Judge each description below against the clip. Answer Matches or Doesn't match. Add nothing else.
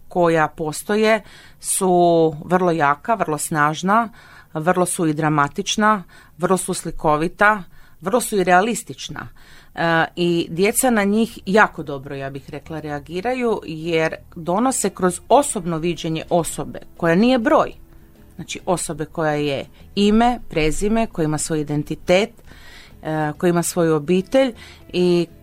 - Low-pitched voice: Doesn't match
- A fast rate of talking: Doesn't match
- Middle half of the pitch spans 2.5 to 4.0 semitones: Doesn't match